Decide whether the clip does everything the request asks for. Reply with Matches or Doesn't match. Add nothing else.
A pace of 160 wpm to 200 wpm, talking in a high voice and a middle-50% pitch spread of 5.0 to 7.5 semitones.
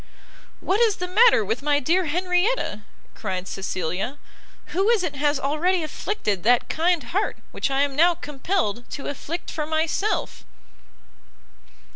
Doesn't match